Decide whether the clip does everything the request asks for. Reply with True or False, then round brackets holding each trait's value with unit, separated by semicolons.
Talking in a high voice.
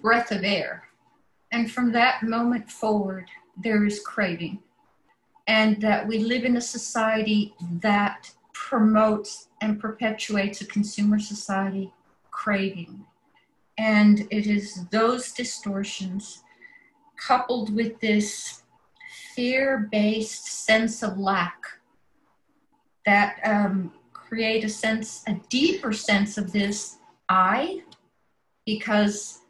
True (215 Hz)